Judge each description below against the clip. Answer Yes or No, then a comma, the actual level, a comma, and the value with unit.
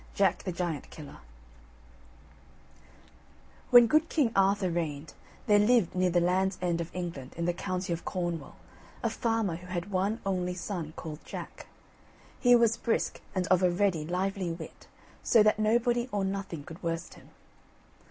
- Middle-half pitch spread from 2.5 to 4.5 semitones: Yes, average, 3.3 semitones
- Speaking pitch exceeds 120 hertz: Yes, medium, 185 Hz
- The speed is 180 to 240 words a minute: No, average, 160 wpm